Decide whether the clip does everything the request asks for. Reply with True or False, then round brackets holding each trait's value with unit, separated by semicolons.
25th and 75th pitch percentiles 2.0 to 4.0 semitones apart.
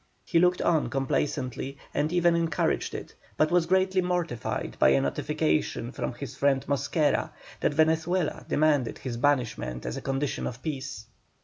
False (4.4 semitones)